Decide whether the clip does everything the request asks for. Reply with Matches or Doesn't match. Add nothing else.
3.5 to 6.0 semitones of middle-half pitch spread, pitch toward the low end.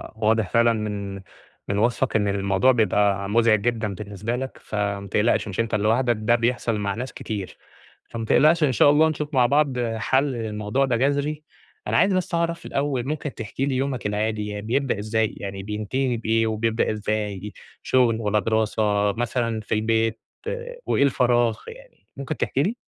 Matches